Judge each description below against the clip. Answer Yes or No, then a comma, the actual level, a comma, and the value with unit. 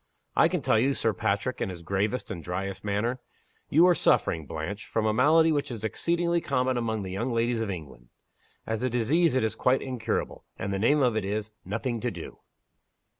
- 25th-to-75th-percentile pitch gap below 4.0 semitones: No, average, 4.5 semitones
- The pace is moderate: No, fast, 210 wpm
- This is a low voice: Yes, low, 110 Hz